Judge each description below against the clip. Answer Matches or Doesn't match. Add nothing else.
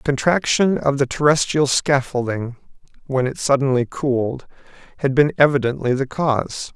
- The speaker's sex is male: Matches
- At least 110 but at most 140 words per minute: Matches